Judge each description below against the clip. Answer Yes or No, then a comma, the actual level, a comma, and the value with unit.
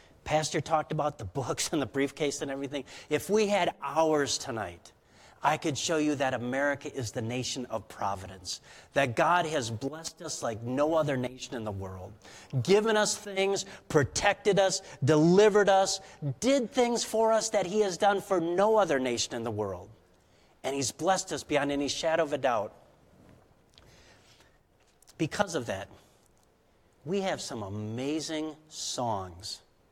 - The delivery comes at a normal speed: Yes, average, 155 wpm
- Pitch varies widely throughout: Yes, wide, 7.0 semitones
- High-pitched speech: No, medium, 145 Hz